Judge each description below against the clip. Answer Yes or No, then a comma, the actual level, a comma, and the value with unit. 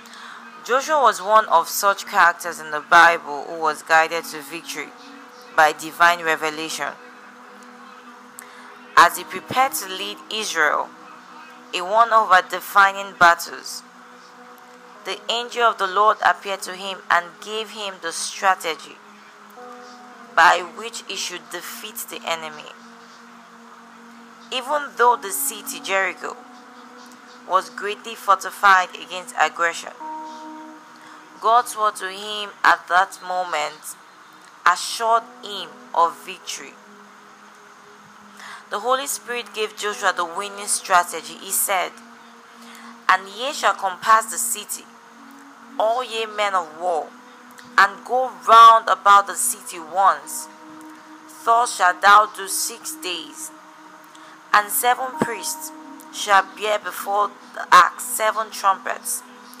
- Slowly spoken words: Yes, slow, 115 wpm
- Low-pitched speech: No, high, 205 Hz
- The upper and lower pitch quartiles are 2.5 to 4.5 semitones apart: No, average, 4.9 semitones